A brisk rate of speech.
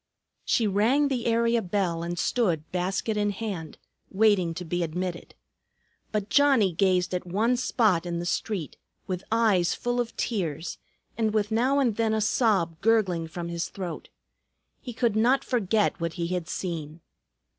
No: average, 160 wpm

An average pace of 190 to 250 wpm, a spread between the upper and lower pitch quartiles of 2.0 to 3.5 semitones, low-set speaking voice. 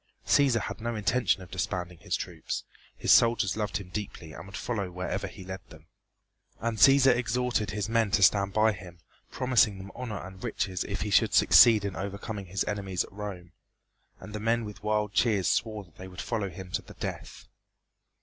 Yes: average, 195 wpm; average, 2.9 semitones; low, 100 Hz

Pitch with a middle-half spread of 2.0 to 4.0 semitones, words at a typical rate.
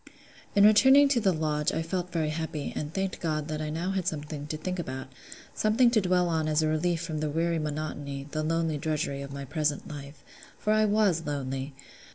No: average, 3.2 semitones; fast, 210 wpm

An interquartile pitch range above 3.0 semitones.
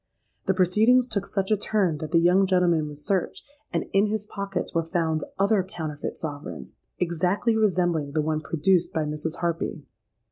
Yes: average, 3.8 semitones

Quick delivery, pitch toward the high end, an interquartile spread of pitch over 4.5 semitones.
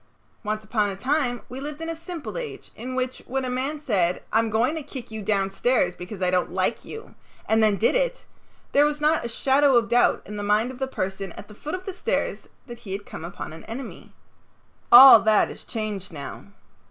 Yes: fast, 220 wpm; high, 235 Hz; average, 5.2 semitones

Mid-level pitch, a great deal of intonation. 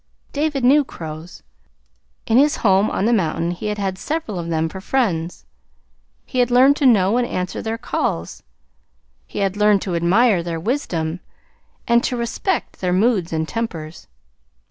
No: high, 200 Hz; wide, 6.1 semitones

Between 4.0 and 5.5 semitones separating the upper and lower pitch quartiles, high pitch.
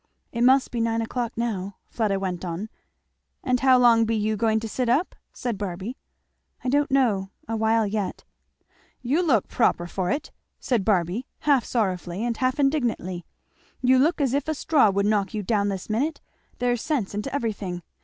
Yes: average, 4.3 semitones; high, 225 Hz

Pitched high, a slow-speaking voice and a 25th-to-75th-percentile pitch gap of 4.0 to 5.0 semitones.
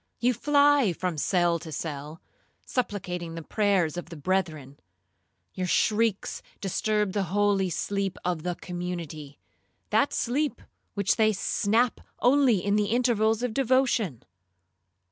Yes: high, 195 Hz; slow, 125 wpm; average, 4.6 semitones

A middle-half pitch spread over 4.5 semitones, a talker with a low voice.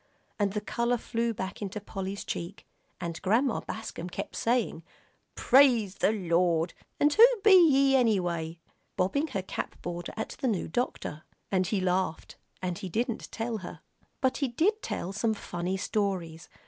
No: average, 4.9 semitones; high, 200 Hz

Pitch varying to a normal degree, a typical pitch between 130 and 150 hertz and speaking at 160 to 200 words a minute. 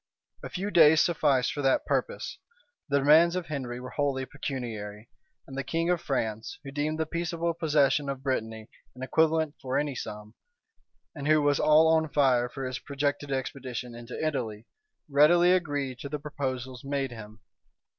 Yes: average, 3.4 semitones; medium, 140 Hz; average, 165 wpm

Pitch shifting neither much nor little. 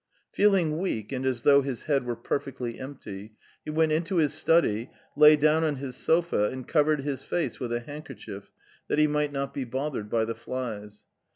Yes: average, 4.3 semitones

